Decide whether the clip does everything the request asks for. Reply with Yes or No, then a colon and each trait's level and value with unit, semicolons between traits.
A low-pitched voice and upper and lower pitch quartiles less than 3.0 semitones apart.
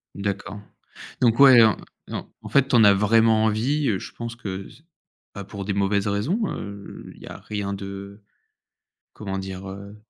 Yes: low, 100 Hz; narrow, 2.4 semitones